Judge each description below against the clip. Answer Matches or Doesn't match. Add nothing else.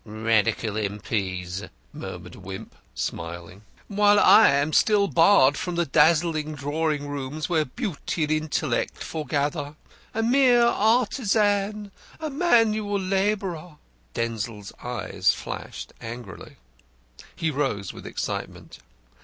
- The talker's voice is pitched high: Doesn't match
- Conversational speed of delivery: Doesn't match